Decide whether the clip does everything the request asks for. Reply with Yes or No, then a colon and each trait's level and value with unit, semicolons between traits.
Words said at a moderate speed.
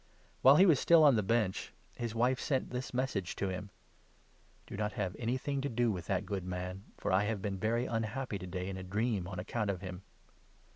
No: fast, 230 wpm